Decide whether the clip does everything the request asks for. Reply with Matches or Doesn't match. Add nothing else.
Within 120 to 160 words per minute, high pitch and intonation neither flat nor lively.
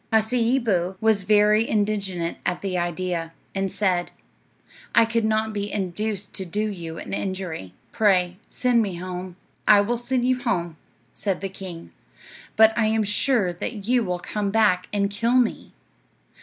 Matches